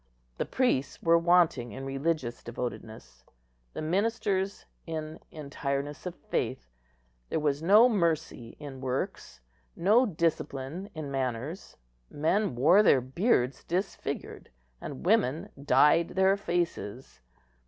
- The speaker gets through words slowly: Yes, slow, 110 wpm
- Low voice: No, medium, 155 Hz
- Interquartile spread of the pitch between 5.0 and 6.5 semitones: Yes, wide, 5.5 semitones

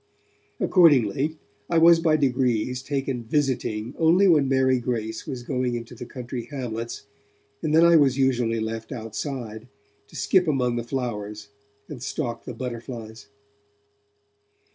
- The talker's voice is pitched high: No, low, 125 Hz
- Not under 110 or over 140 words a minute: Yes, slow, 135 wpm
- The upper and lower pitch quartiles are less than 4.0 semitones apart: Yes, average, 3.6 semitones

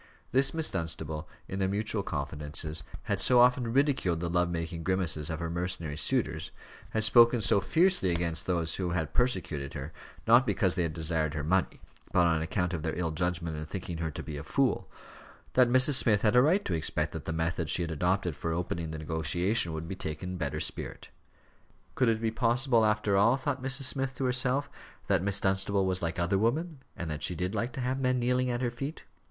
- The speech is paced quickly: Yes, fast, 215 wpm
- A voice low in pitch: Yes, very low, 90 Hz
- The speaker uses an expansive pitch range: Yes, wide, 6.7 semitones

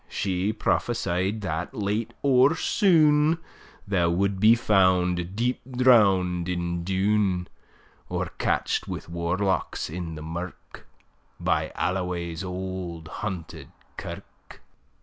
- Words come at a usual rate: No, slow, 105 wpm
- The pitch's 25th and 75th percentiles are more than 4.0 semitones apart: No, average, 3.5 semitones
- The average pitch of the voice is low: Yes, very low, 95 Hz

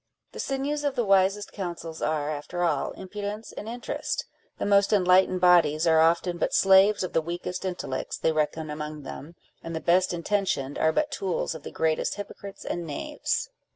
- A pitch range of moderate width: Yes, average, 3.8 semitones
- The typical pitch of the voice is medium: Yes, medium, 180 Hz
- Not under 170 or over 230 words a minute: Yes, average, 180 wpm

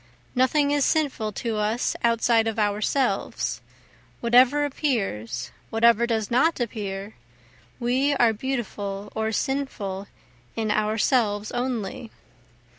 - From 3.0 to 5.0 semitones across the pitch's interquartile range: Yes, average, 3.6 semitones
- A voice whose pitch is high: Yes, high, 230 Hz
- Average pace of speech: No, slow, 105 wpm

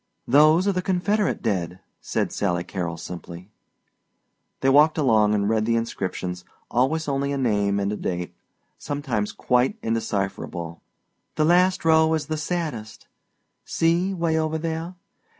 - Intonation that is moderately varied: No, wide, 8.0 semitones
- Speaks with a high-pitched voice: No, low, 135 Hz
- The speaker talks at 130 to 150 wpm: Yes, average, 140 wpm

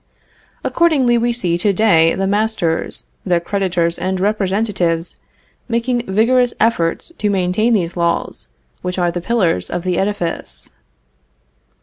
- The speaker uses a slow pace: Yes, slow, 125 wpm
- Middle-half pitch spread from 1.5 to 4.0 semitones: No, average, 4.5 semitones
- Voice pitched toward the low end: No, high, 190 Hz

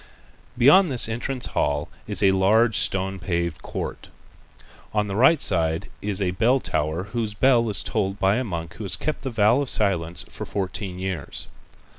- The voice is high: No, low, 100 Hz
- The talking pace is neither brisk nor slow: Yes, average, 175 wpm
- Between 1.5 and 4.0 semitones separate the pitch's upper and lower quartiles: No, average, 4.4 semitones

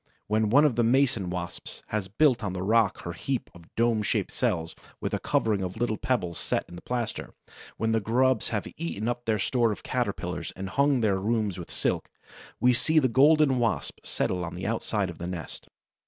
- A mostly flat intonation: No, average, 4.7 semitones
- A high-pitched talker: No, low, 110 Hz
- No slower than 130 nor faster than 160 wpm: No, fast, 205 wpm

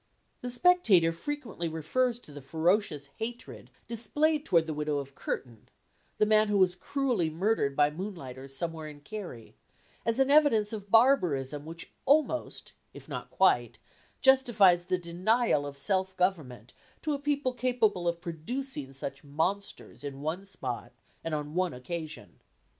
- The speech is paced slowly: No, average, 145 wpm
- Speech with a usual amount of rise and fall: No, wide, 7.6 semitones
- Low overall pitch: No, medium, 180 Hz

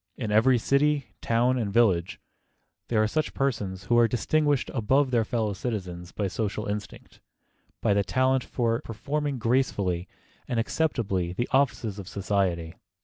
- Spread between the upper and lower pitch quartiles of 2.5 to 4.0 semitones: No, average, 4.6 semitones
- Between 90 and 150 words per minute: Yes, average, 145 wpm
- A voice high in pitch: No, low, 115 Hz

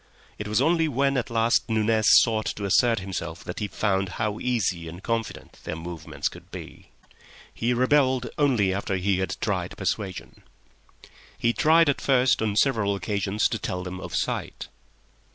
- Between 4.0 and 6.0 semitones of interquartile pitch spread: Yes, average, 4.4 semitones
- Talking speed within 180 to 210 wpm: No, average, 165 wpm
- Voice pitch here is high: No, low, 110 Hz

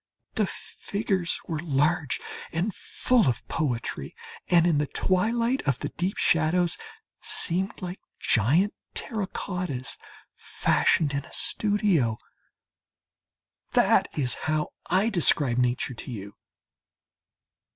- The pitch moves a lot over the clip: Yes, wide, 5.7 semitones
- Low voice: No, medium, 165 Hz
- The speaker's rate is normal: No, slow, 110 wpm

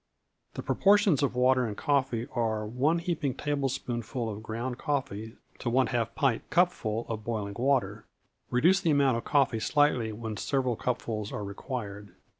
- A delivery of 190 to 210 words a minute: No, average, 155 wpm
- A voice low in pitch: Yes, low, 125 Hz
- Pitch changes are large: No, average, 4.0 semitones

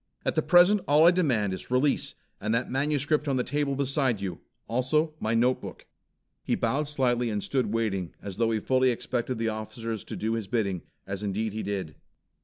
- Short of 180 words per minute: No, average, 195 wpm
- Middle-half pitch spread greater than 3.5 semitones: Yes, average, 4.5 semitones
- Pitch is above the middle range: No, low, 120 Hz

